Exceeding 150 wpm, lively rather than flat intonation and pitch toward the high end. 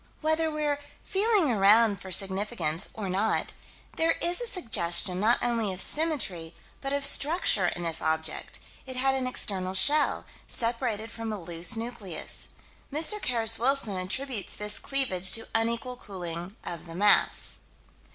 No: average, 145 wpm; wide, 6.5 semitones; high, 225 Hz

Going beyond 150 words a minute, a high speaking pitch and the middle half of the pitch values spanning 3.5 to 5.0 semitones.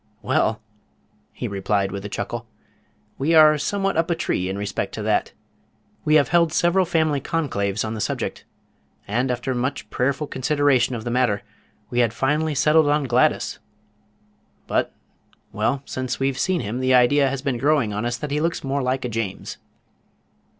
No: average, 170 wpm; low, 130 Hz; average, 4.5 semitones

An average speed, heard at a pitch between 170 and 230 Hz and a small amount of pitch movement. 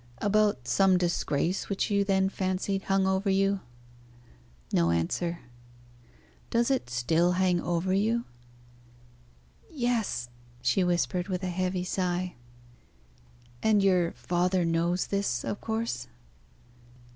No: slow, 110 wpm; medium, 185 Hz; narrow, 2.3 semitones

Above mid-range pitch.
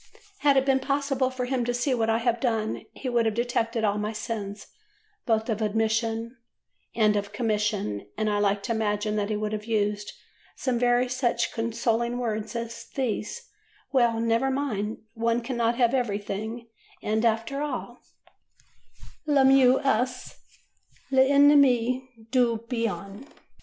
Yes: high, 230 Hz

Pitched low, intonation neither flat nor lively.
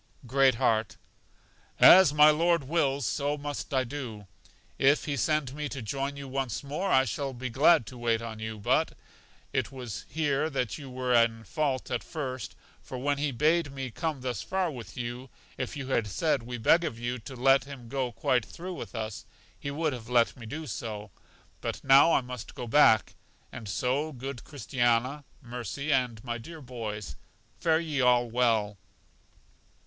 Yes: low, 130 Hz; average, 3.5 semitones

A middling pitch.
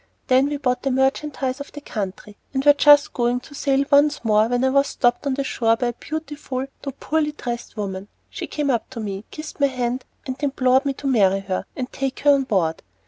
No: very high, 260 Hz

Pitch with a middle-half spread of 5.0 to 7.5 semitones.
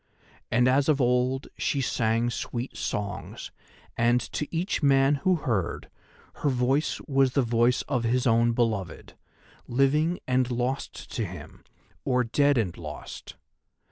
No: average, 2.7 semitones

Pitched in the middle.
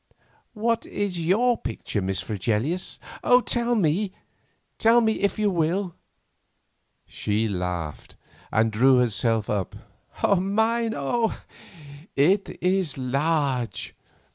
Yes: medium, 165 Hz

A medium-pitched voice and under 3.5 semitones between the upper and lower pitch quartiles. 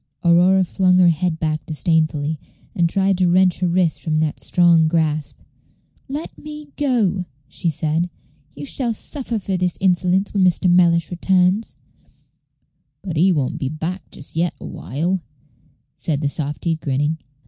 Yes: medium, 175 Hz; average, 3.1 semitones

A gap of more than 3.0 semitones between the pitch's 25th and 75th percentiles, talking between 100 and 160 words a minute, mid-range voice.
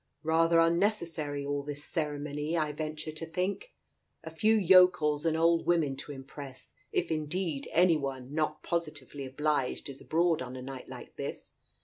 No: average, 2.7 semitones; average, 155 wpm; medium, 155 Hz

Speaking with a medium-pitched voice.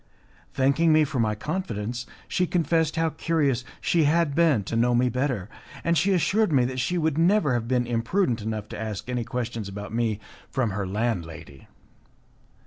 No: low, 125 Hz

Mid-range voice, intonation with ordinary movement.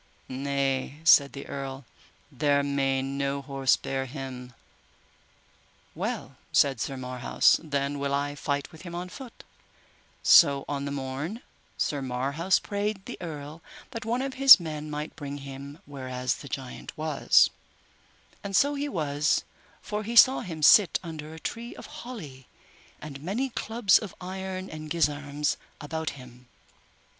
Yes: medium, 145 Hz; average, 4.7 semitones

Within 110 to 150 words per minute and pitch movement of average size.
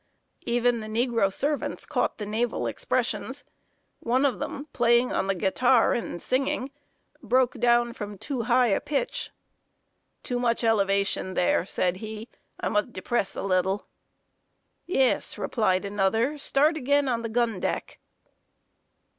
Yes: average, 140 wpm; average, 3.7 semitones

